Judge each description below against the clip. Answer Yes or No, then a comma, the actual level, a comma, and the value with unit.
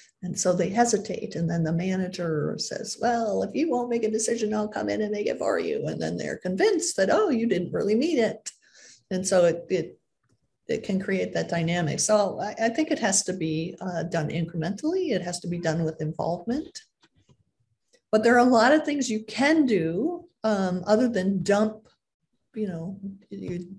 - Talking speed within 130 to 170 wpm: No, average, 200 wpm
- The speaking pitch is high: Yes, high, 200 Hz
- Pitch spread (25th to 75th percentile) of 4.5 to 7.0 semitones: Yes, average, 5.0 semitones